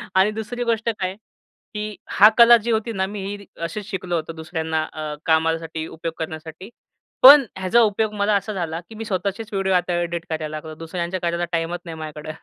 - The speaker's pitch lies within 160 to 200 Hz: Yes, medium, 185 Hz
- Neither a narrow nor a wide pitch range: Yes, average, 4.4 semitones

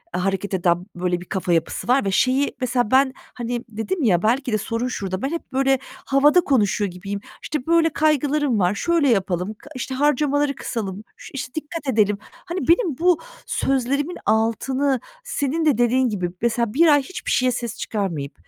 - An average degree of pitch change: No, wide, 5.9 semitones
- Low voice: No, very high, 250 Hz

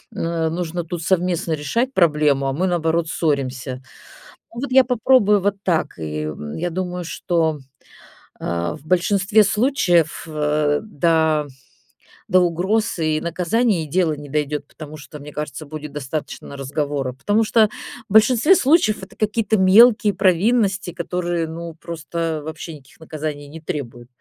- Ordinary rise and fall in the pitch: Yes, average, 4.5 semitones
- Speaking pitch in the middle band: Yes, medium, 165 Hz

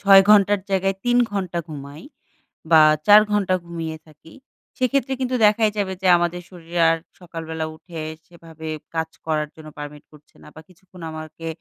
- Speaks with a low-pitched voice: No, medium, 170 Hz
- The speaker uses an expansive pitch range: No, average, 3.5 semitones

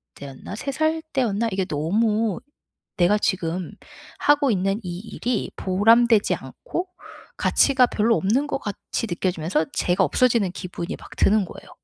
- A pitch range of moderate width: Yes, average, 4.8 semitones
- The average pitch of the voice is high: Yes, high, 210 Hz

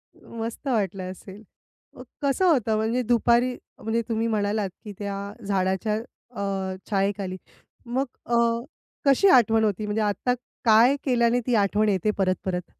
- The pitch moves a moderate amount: Yes, average, 3.0 semitones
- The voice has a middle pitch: No, high, 215 Hz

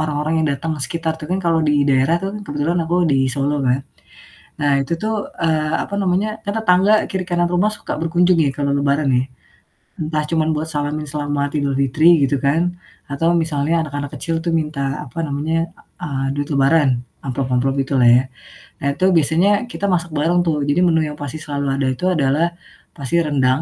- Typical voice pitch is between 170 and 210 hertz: No, medium, 150 Hz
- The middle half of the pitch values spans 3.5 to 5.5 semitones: No, average, 3.0 semitones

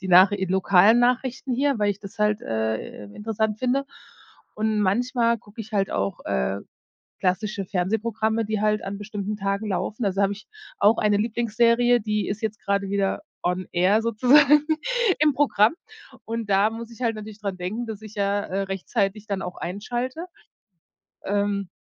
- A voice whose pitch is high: Yes, high, 210 Hz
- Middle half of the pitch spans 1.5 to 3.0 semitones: Yes, average, 2.7 semitones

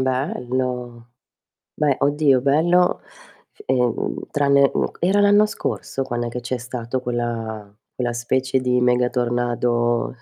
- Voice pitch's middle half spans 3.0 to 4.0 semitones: No, narrow, 2.4 semitones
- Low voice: Yes, low, 125 Hz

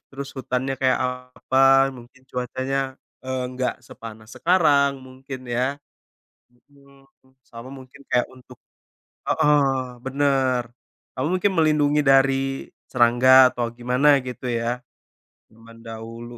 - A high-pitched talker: No, low, 130 Hz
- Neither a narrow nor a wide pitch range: No, narrow, 1.7 semitones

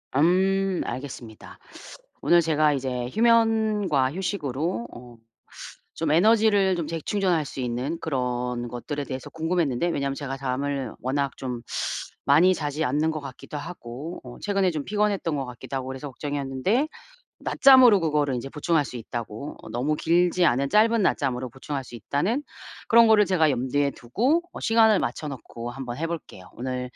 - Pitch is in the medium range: Yes, medium, 145 Hz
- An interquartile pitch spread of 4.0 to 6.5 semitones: Yes, wide, 6.0 semitones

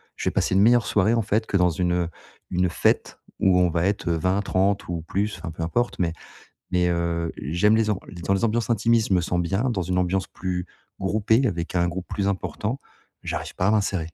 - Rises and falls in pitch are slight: No, average, 3.2 semitones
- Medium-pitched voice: No, very low, 95 Hz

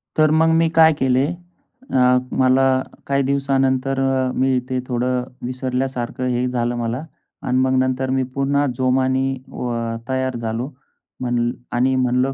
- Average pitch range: No, narrow, 1.1 semitones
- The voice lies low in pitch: Yes, low, 130 Hz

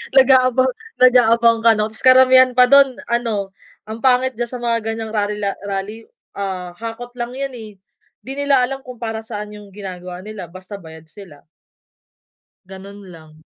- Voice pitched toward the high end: Yes, high, 225 Hz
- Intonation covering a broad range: No, average, 4.1 semitones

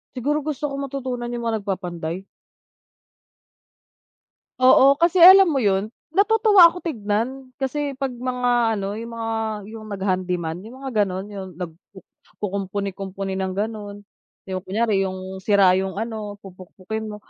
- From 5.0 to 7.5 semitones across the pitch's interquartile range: Yes, average, 5.3 semitones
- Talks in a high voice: Yes, high, 215 Hz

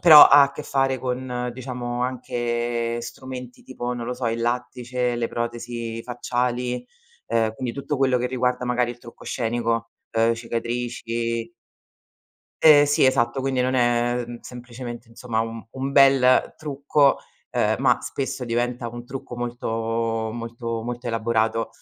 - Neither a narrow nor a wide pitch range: No, narrow, 1.5 semitones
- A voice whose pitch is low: Yes, low, 120 Hz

